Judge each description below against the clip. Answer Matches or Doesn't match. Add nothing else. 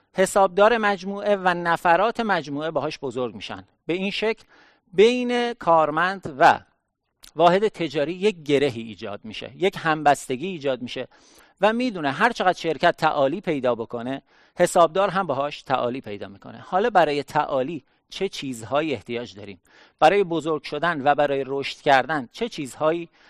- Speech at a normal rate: Matches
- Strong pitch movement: Matches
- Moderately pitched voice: Matches